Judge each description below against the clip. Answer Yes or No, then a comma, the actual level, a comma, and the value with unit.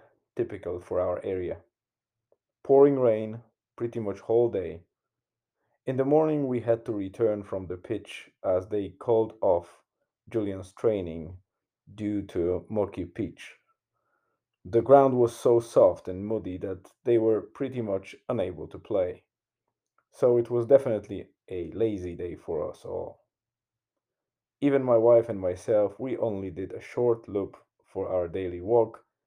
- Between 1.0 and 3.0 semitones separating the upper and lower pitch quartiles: No, average, 4.0 semitones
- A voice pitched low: Yes, low, 110 Hz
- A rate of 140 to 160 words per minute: Yes, average, 145 wpm